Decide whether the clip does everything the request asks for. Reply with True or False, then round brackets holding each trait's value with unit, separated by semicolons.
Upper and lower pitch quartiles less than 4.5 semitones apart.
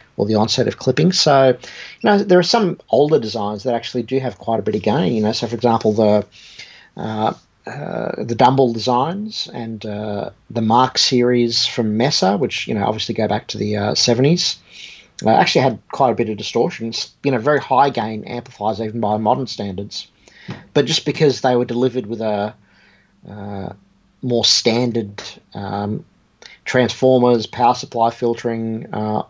True (3.1 semitones)